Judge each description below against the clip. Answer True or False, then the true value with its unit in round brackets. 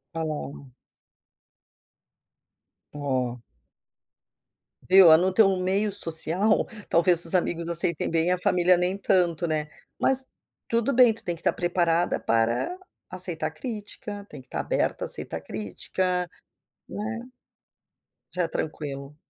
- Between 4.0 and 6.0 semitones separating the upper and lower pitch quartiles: False (3.6 semitones)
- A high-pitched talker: False (175 Hz)